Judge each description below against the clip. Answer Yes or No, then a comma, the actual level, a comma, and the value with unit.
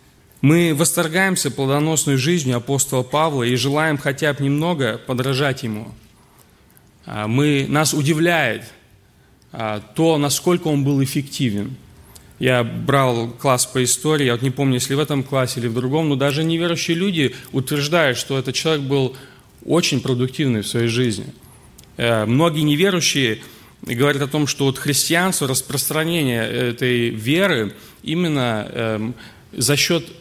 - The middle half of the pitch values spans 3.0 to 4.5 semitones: Yes, average, 3.8 semitones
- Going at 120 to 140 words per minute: Yes, average, 130 wpm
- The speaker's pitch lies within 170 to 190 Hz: No, low, 135 Hz